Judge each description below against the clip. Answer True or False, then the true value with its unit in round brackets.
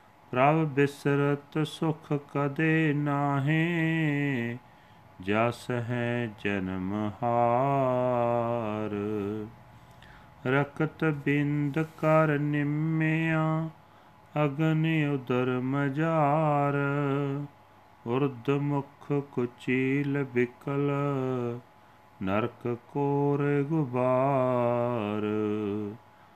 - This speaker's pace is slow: True (50 wpm)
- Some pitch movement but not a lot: True (3.3 semitones)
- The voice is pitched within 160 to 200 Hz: False (140 Hz)